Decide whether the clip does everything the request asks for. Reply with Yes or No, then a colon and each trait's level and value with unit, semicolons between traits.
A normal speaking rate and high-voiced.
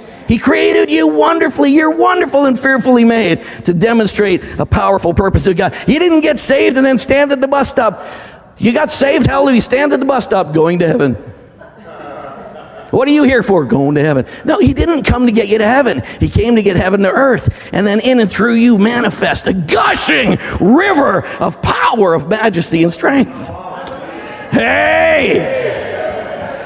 Yes: average, 180 wpm; high, 235 Hz